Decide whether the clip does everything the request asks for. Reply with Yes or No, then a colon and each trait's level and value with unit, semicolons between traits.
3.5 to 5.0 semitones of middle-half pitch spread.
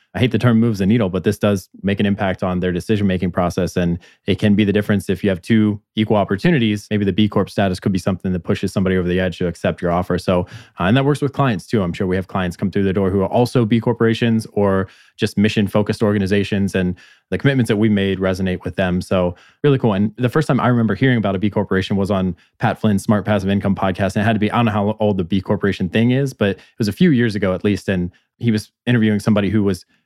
No: average, 2.7 semitones